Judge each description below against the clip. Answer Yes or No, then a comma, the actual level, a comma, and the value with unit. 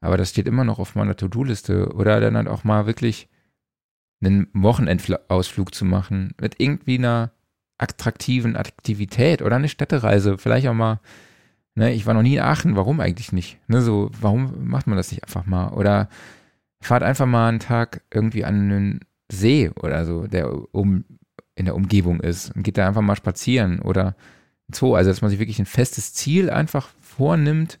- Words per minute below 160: No, average, 180 wpm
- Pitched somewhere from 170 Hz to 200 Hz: No, low, 105 Hz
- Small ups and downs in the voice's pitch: No, average, 4.3 semitones